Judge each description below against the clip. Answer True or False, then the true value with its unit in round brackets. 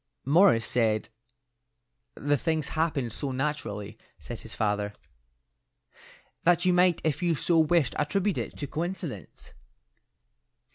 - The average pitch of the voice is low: False (150 Hz)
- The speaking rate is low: True (115 wpm)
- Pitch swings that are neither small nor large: False (6.8 semitones)